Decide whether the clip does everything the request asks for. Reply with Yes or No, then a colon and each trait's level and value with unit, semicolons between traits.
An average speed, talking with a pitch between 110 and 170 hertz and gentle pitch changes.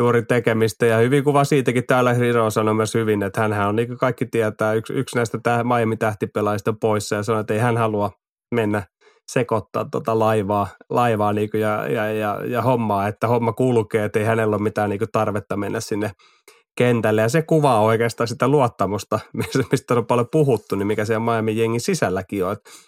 No: fast, 185 wpm; low, 115 Hz; narrow, 2.1 semitones